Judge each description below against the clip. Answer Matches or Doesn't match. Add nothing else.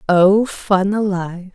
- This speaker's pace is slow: Matches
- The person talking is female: Matches